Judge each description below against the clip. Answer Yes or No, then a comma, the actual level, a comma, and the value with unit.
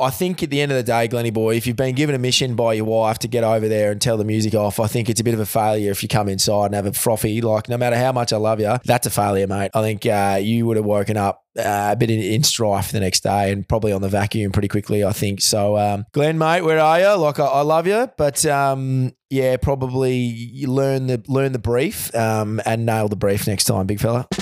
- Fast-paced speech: Yes, fast, 280 wpm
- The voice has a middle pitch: No, low, 115 Hz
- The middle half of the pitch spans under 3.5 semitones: No, average, 3.8 semitones